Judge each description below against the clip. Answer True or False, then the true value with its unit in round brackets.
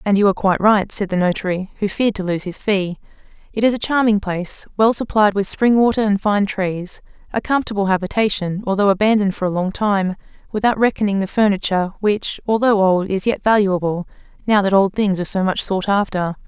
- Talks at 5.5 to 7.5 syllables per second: True (5.9 syllables/s)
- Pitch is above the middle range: True (200 Hz)